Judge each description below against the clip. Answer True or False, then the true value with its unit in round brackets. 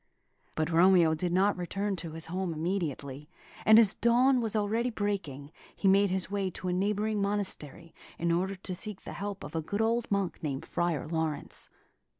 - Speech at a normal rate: True (180 wpm)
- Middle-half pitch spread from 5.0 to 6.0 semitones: False (3.8 semitones)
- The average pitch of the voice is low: False (190 Hz)